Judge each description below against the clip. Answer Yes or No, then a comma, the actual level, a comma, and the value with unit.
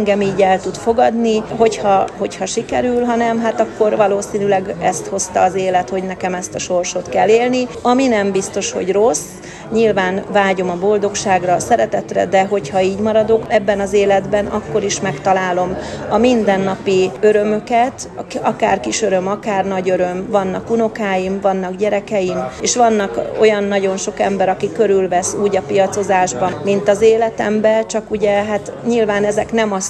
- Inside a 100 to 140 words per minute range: No, fast, 155 wpm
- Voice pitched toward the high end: Yes, high, 200 Hz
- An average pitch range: No, narrow, 2.3 semitones